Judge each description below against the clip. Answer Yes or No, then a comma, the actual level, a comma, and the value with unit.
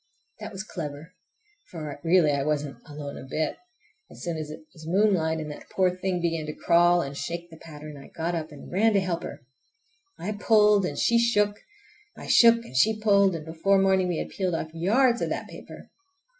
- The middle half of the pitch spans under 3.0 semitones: No, average, 4.3 semitones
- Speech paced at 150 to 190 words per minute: No, fast, 205 wpm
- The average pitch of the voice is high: No, medium, 170 Hz